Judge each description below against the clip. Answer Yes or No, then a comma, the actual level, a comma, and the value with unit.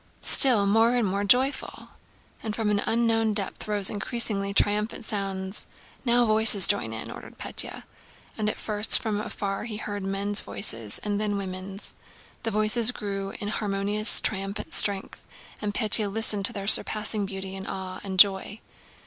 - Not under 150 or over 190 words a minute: Yes, average, 155 wpm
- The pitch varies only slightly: Yes, narrow, 1.7 semitones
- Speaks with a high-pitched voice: Yes, high, 205 Hz